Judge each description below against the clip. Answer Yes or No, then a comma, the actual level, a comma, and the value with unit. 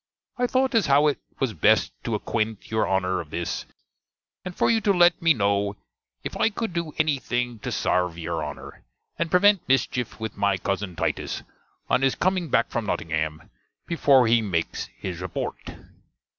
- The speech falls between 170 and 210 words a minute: Yes, average, 175 wpm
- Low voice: Yes, low, 120 Hz